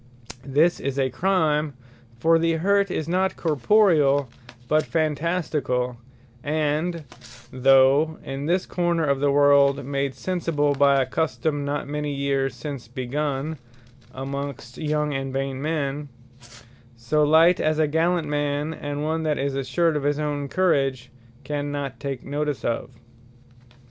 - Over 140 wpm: No, slow, 135 wpm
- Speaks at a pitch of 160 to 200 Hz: No, medium, 145 Hz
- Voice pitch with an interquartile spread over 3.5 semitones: No, narrow, 2.5 semitones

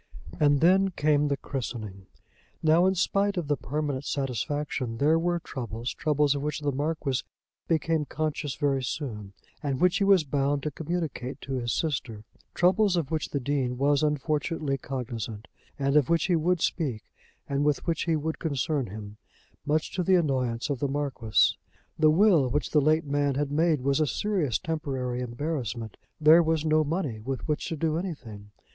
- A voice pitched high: No, medium, 145 Hz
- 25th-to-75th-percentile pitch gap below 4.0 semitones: Yes, average, 3.4 semitones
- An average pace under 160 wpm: No, average, 175 wpm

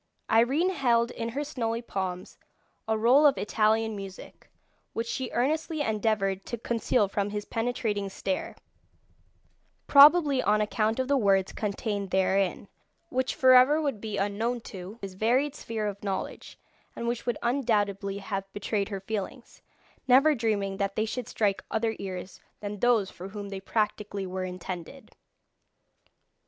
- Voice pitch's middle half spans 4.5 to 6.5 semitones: No, average, 3.8 semitones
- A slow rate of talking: No, average, 145 wpm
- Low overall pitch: No, high, 220 Hz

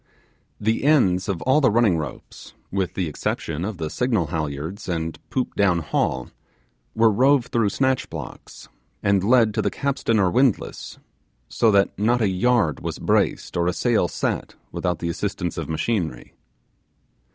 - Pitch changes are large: Yes, wide, 5.7 semitones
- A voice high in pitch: No, low, 100 Hz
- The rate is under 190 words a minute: Yes, average, 160 wpm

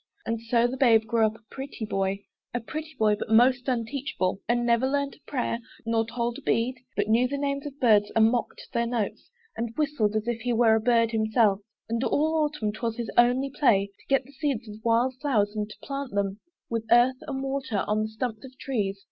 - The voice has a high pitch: Yes, high, 235 Hz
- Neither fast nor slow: No, fast, 220 wpm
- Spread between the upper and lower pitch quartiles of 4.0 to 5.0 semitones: No, average, 3.2 semitones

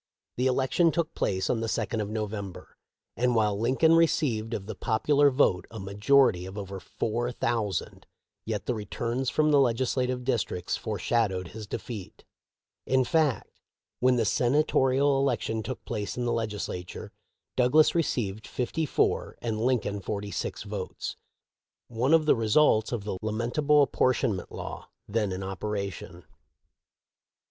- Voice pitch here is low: Yes, low, 115 Hz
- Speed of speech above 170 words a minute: No, average, 150 wpm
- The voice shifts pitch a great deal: No, average, 4.1 semitones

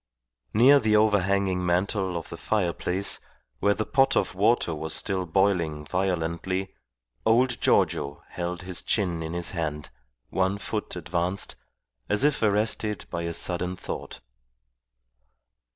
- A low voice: Yes, very low, 95 Hz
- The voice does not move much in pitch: No, average, 3.4 semitones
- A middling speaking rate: No, slow, 130 wpm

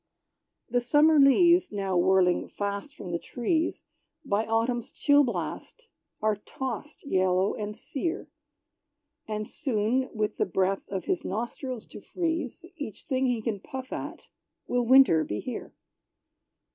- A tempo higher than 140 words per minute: No, slow, 135 wpm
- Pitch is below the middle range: No, high, 230 Hz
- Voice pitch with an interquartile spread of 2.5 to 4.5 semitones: No, average, 5.3 semitones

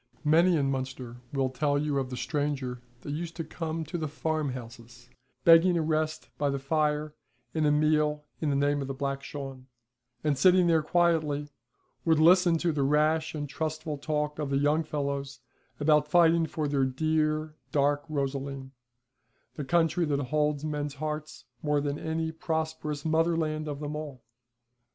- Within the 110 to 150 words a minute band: No, average, 165 wpm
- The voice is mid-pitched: Yes, medium, 150 Hz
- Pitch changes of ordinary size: No, narrow, 2.1 semitones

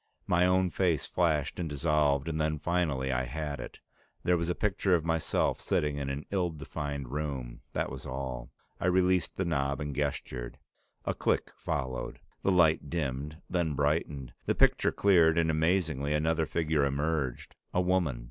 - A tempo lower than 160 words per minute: No, average, 165 wpm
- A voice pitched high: No, very low, 75 Hz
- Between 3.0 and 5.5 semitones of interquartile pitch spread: Yes, average, 3.6 semitones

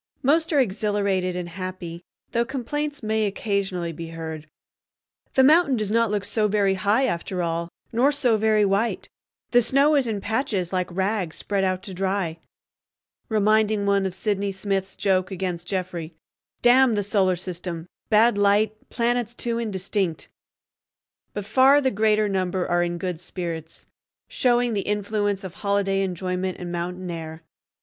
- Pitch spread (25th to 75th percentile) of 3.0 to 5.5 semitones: Yes, average, 3.3 semitones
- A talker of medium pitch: No, high, 200 Hz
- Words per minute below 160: Yes, average, 150 wpm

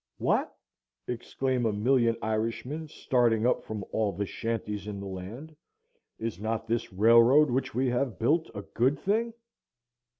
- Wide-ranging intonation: No, average, 3.4 semitones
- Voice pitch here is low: Yes, low, 115 Hz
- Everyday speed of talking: Yes, average, 145 wpm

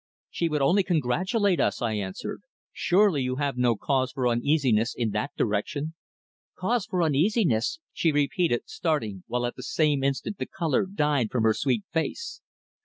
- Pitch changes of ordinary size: No, wide, 6.0 semitones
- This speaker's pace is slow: No, average, 165 wpm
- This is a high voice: No, medium, 140 Hz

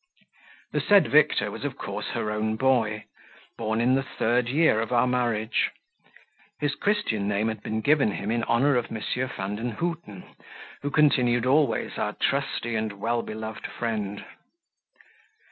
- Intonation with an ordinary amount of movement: Yes, average, 3.4 semitones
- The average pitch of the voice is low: Yes, low, 115 Hz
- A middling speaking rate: Yes, average, 145 wpm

